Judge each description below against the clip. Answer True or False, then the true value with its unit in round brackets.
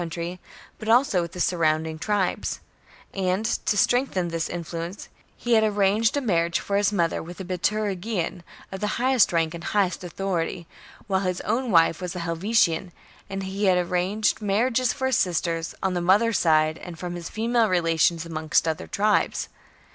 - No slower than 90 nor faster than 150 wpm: False (170 wpm)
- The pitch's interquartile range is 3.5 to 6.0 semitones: True (3.8 semitones)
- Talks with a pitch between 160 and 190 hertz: True (185 Hz)